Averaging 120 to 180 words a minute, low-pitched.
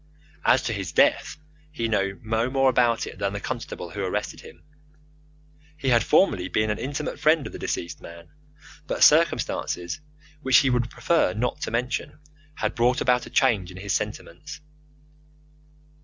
Yes: average, 165 wpm; low, 115 Hz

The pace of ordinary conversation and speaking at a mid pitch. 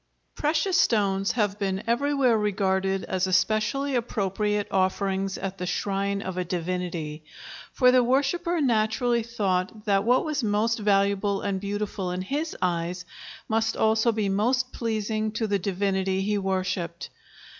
No: average, 145 wpm; high, 205 Hz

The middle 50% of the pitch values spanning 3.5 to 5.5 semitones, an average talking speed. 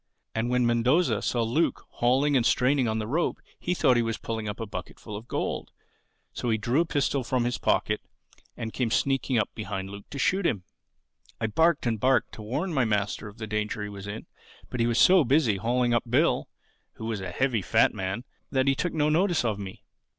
No: average, 4.0 semitones; fast, 215 wpm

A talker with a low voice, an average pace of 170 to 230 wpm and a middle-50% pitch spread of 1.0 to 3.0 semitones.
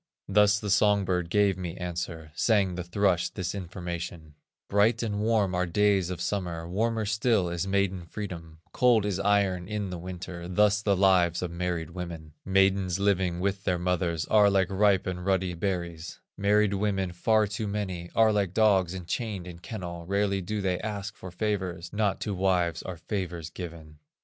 Yes: very low, 95 Hz; average, 175 wpm; average, 2.7 semitones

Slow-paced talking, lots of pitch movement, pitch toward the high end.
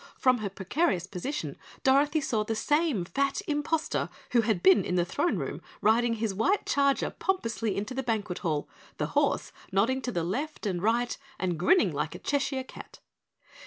No: average, 175 wpm; wide, 6.1 semitones; high, 230 Hz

